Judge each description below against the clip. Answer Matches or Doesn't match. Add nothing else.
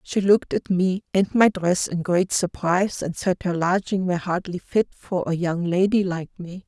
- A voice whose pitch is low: Doesn't match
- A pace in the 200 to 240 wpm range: Matches